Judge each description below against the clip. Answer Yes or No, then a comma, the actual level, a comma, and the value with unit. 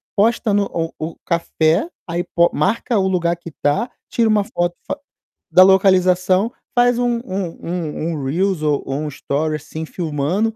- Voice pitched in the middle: Yes, medium, 175 Hz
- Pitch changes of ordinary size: Yes, average, 4.0 semitones